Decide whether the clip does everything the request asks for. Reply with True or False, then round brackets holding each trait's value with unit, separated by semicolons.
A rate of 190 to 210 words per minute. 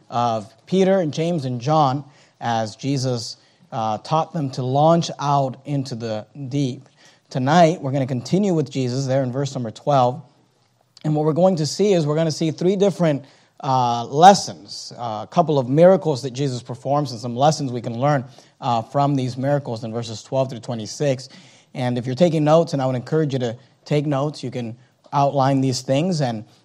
True (195 wpm)